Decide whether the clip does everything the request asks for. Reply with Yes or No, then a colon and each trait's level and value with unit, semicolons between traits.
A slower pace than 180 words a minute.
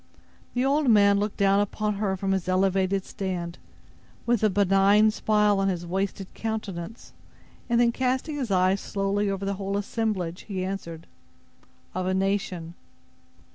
Yes: average, 150 wpm